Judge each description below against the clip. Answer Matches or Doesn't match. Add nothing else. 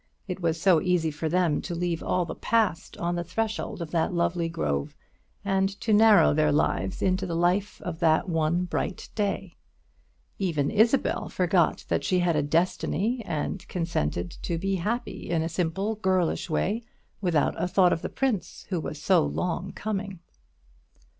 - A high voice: Doesn't match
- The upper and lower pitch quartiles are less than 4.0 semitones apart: Matches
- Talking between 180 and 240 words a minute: Doesn't match